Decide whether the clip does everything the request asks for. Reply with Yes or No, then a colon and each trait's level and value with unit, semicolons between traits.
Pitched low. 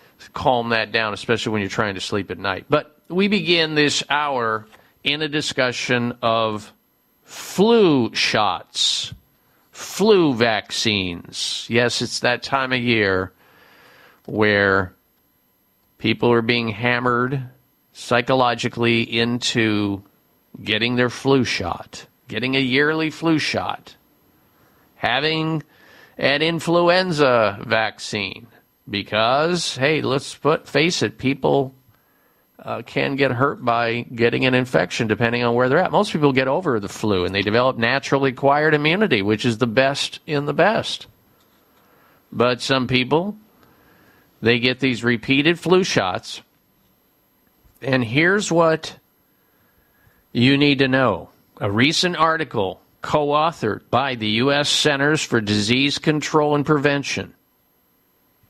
Yes: low, 125 Hz